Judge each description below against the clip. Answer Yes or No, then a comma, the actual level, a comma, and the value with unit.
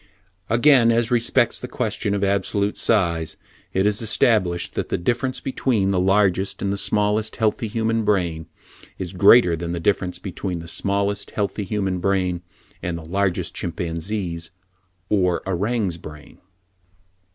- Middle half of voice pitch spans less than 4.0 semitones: Yes, average, 3.6 semitones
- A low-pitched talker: Yes, low, 100 Hz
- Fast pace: No, average, 140 wpm